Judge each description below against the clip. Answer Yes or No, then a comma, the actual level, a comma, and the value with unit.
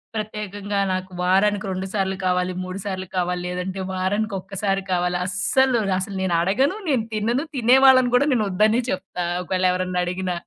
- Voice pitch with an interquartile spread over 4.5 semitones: No, average, 2.8 semitones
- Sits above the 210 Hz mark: No, high, 195 Hz